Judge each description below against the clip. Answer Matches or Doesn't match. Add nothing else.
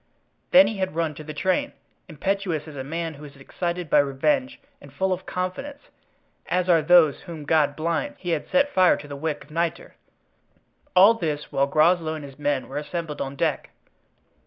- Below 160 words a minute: Doesn't match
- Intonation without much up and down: Doesn't match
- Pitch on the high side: Doesn't match